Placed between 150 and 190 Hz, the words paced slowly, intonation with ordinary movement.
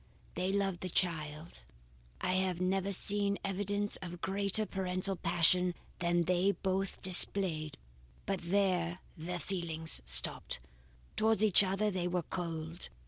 No: medium, 185 Hz; slow, 130 wpm; narrow, 2.2 semitones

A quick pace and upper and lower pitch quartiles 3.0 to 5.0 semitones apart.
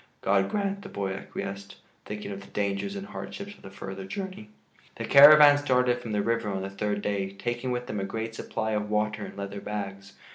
Yes: fast, 210 wpm; average, 4.0 semitones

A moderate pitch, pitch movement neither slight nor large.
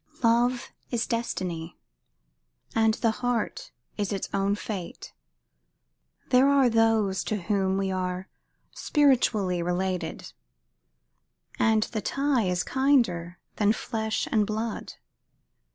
No: high, 215 Hz; average, 3.8 semitones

